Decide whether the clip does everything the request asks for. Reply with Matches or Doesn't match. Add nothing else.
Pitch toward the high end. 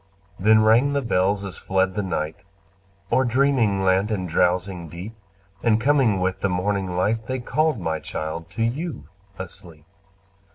Doesn't match